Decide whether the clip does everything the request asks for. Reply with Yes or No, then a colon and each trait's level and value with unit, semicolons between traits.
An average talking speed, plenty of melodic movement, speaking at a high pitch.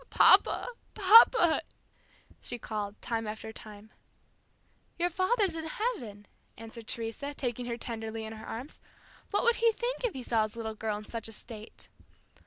Yes: average, 160 wpm; wide, 8.0 semitones; high, 230 Hz